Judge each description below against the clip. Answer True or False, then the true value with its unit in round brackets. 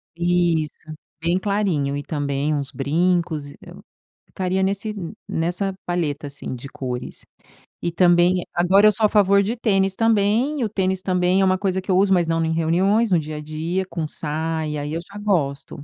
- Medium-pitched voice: True (175 Hz)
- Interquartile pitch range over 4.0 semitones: False (3.7 semitones)